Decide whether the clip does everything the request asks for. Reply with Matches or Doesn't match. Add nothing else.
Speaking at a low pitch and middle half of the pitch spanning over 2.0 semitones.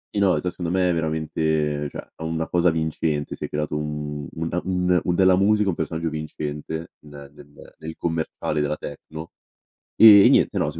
Matches